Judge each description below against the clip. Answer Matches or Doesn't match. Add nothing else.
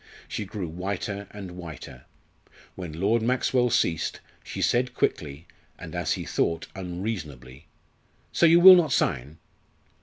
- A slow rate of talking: Matches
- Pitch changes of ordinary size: Doesn't match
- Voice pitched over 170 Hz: Doesn't match